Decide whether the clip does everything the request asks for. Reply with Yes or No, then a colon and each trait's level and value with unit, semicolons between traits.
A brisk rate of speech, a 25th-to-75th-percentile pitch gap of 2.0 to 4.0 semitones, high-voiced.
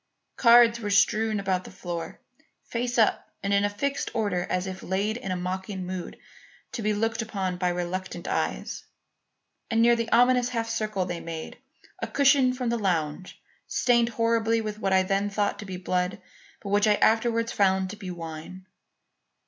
No: average, 180 wpm; average, 3.7 semitones; high, 205 Hz